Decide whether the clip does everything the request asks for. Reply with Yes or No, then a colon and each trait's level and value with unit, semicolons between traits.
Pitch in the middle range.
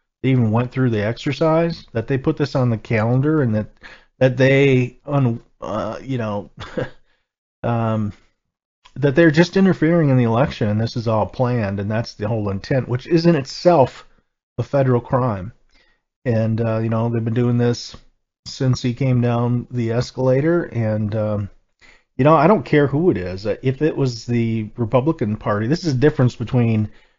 No: low, 125 Hz